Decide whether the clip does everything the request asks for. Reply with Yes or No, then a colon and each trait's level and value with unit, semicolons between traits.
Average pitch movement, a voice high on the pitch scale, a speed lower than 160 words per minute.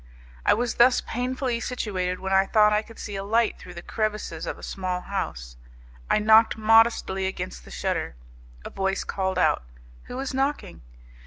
No: average, 3.6 semitones; high, 210 Hz; average, 175 wpm